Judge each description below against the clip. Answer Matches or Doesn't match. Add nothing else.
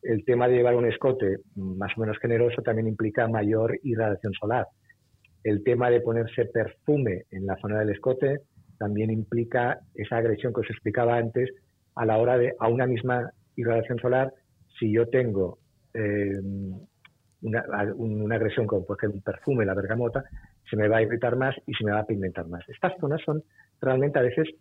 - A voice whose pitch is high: Doesn't match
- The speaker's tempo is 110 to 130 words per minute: Doesn't match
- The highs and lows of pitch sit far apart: Doesn't match